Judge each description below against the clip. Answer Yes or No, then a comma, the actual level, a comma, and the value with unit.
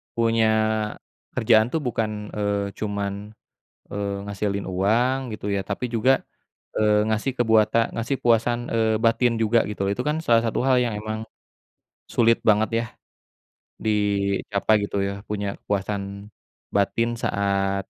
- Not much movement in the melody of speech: Yes, narrow, 2.2 semitones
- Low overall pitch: Yes, low, 110 Hz